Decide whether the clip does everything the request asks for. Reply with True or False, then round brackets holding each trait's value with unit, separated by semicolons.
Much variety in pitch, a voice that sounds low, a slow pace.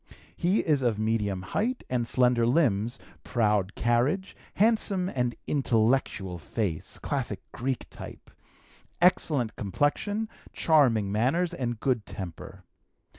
True (6.4 semitones; 120 Hz; 110 wpm)